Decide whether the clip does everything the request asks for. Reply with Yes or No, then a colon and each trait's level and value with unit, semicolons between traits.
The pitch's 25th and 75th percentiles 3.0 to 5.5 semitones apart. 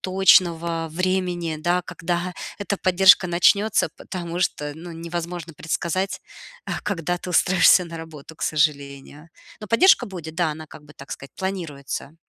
No: narrow, 2.5 semitones